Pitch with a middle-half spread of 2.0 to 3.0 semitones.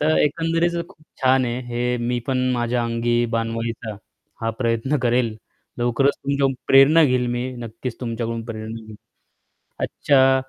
Yes: narrow, 2.6 semitones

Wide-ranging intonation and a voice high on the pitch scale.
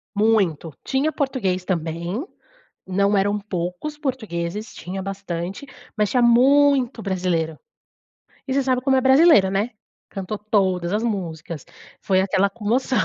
Yes: wide, 5.7 semitones; high, 200 Hz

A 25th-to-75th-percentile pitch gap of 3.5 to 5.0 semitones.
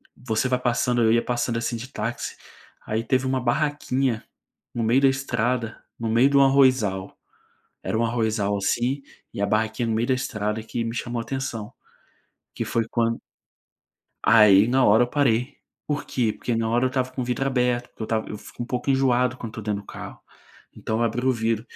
No: narrow, 2.4 semitones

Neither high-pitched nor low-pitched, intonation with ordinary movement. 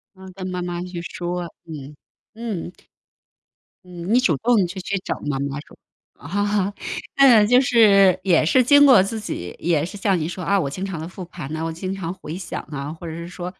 Yes: medium, 180 Hz; average, 3.4 semitones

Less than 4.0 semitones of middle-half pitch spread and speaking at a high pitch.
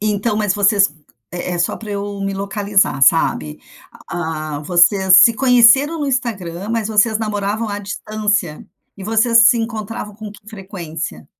Yes: average, 2.8 semitones; high, 205 Hz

